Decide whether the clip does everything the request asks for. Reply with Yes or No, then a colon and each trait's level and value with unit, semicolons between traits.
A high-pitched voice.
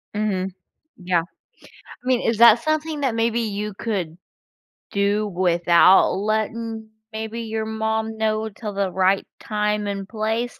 Yes: high, 215 Hz